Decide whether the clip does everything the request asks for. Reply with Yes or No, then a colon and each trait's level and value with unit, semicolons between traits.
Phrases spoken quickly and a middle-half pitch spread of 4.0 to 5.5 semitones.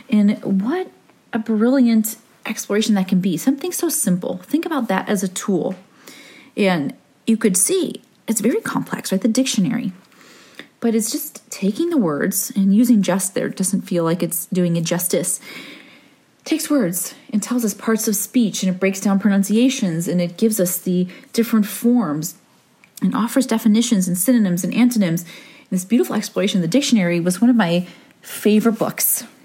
No: average, 175 wpm; average, 4.5 semitones